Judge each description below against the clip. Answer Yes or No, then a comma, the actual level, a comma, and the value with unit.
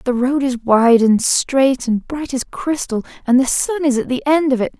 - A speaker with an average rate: No, fast, 240 wpm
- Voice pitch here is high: Yes, very high, 260 Hz